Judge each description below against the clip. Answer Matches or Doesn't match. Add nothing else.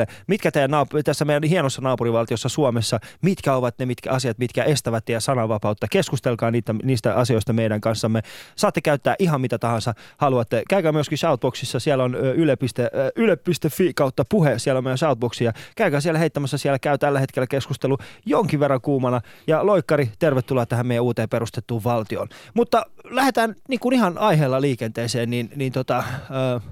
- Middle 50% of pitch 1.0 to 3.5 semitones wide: Doesn't match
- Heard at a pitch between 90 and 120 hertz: Doesn't match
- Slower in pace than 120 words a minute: Doesn't match